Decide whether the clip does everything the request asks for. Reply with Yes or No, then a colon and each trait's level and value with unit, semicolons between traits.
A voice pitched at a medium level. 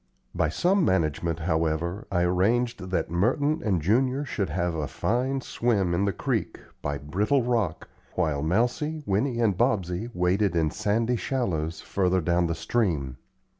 No: very low, 95 Hz